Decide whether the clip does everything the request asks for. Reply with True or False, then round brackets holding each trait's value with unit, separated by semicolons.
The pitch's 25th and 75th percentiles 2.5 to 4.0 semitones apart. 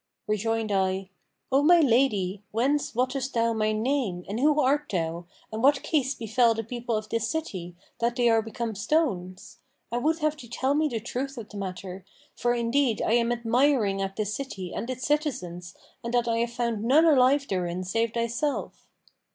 False (4.5 semitones)